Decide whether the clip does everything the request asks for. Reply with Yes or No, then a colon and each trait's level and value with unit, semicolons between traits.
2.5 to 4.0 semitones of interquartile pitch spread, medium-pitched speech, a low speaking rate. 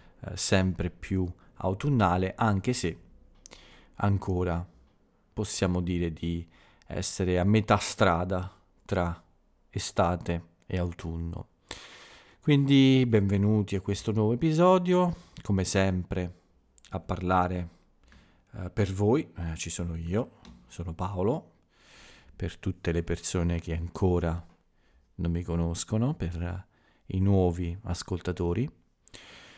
No: average, 2.9 semitones; very low, 90 Hz; slow, 100 wpm